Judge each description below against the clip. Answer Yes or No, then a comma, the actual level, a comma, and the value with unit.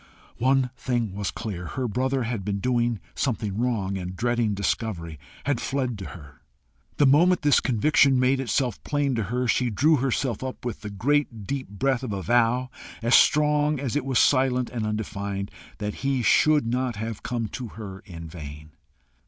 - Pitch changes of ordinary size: Yes, average, 4.4 semitones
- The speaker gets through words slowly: No, average, 175 wpm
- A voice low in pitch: Yes, low, 120 Hz